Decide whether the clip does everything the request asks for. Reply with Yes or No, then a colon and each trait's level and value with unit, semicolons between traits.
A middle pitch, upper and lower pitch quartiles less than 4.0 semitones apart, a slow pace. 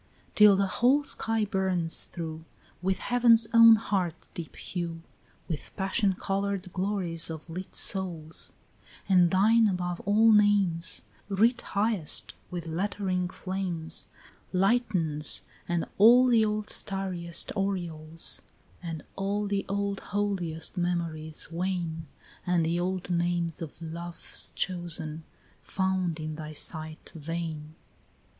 Yes: medium, 180 Hz; average, 3.4 semitones; slow, 120 wpm